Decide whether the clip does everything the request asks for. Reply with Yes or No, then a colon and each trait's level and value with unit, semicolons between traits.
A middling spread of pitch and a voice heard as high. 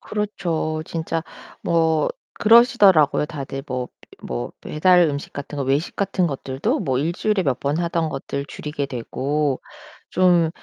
No: average, 3.9 semitones; medium, 155 Hz